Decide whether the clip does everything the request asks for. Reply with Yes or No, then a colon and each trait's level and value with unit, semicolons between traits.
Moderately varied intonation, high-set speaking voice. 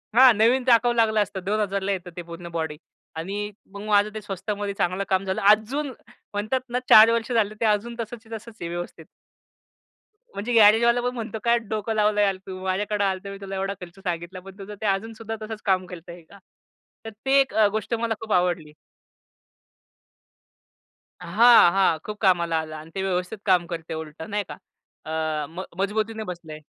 Yes: average, 3.3 semitones; high, 205 Hz